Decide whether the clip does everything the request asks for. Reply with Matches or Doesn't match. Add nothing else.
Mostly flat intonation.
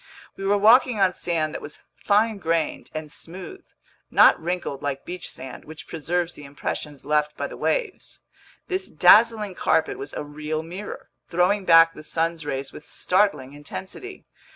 Doesn't match